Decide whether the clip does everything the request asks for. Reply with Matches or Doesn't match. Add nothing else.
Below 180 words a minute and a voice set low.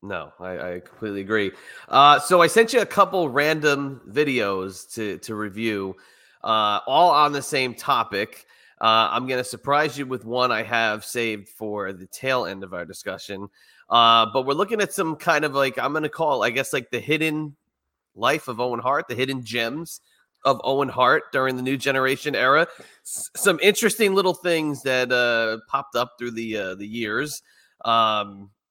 Doesn't match